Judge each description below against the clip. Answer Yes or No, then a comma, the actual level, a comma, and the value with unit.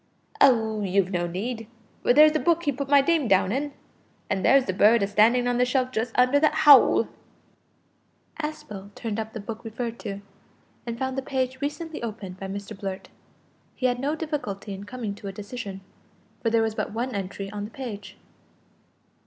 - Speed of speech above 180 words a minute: Yes, average, 190 wpm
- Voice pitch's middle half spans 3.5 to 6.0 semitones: Yes, average, 4.6 semitones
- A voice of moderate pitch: No, high, 230 Hz